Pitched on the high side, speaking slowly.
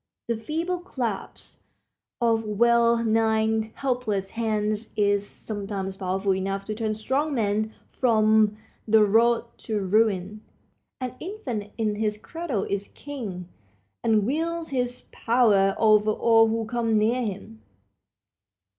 Yes: high, 220 Hz; slow, 120 wpm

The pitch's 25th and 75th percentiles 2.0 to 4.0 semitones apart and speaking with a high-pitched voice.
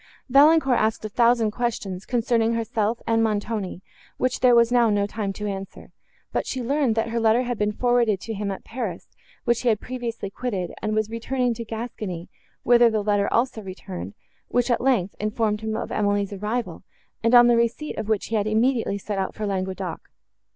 Yes: average, 2.7 semitones; high, 225 Hz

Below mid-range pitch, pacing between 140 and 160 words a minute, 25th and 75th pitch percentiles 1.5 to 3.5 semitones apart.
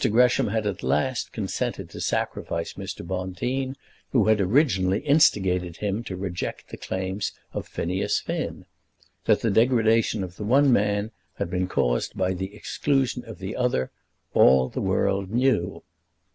No: low, 100 Hz; average, 150 wpm; average, 4.6 semitones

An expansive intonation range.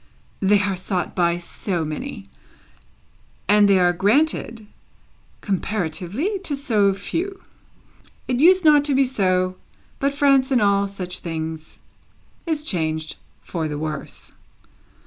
Yes: wide, 7.7 semitones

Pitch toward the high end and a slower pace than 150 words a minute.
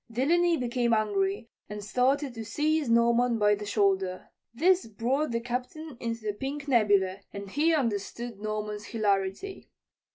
Yes: high, 230 Hz; average, 140 wpm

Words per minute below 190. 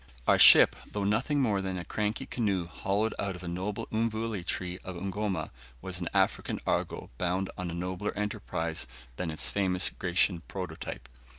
Yes: average, 170 wpm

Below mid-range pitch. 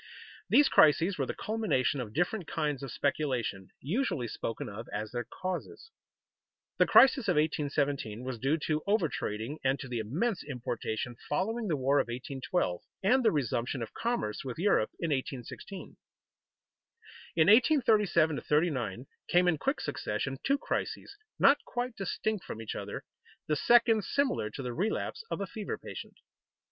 No: medium, 150 Hz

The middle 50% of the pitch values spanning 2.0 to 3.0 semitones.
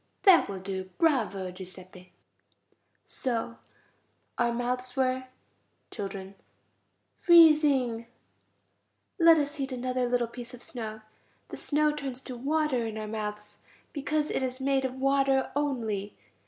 No: average, 4.3 semitones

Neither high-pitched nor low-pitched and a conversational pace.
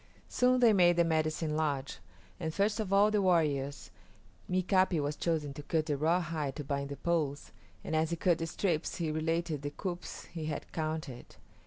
Yes: medium, 160 Hz; average, 185 wpm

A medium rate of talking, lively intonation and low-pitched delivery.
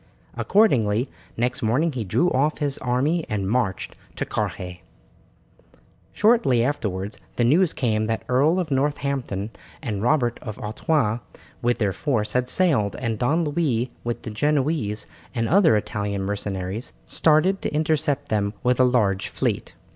Yes: average, 145 wpm; wide, 5.7 semitones; low, 125 Hz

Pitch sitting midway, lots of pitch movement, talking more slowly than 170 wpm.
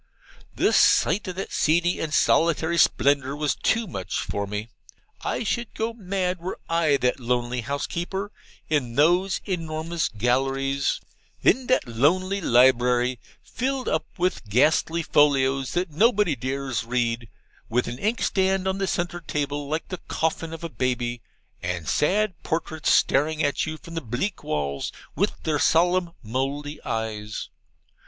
Yes: medium, 150 Hz; wide, 6.1 semitones; average, 145 wpm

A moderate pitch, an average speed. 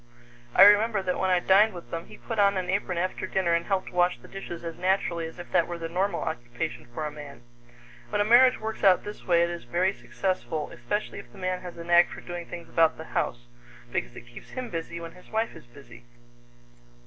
No: medium, 175 Hz; fast, 230 wpm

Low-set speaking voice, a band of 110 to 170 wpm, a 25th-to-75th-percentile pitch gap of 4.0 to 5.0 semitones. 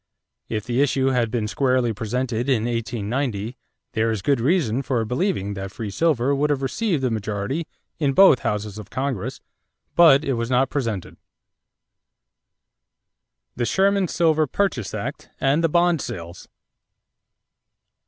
Yes: low, 125 Hz; average, 140 wpm; average, 4.6 semitones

